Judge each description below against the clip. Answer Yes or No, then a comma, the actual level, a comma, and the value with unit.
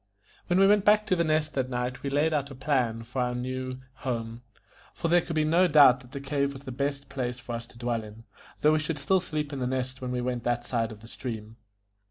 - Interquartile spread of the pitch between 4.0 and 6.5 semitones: No, average, 3.6 semitones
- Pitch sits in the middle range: No, low, 130 Hz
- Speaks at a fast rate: Yes, fast, 265 wpm